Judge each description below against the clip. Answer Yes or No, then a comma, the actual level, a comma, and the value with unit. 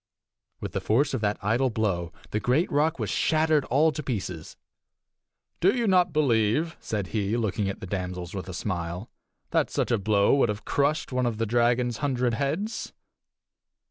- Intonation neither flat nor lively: No, wide, 6.0 semitones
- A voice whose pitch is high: No, low, 120 Hz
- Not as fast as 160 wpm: No, average, 175 wpm